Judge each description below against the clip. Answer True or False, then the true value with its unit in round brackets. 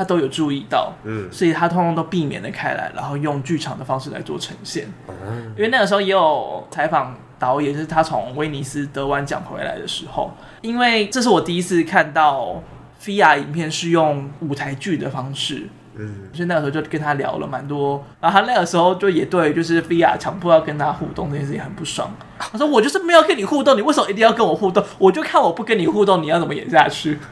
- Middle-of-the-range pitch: True (160 Hz)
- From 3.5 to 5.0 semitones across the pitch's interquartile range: False (5.6 semitones)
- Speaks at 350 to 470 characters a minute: True (355 characters per minute)